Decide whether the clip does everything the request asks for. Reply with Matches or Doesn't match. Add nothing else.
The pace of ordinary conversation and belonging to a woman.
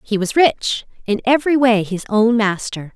Matches